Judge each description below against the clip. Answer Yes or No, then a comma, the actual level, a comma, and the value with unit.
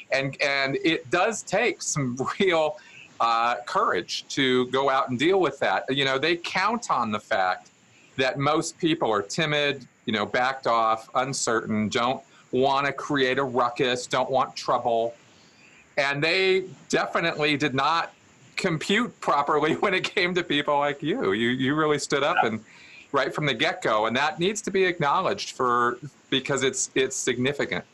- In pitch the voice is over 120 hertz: Yes, medium, 140 Hz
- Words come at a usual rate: Yes, average, 165 wpm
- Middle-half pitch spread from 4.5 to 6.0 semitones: No, average, 3.7 semitones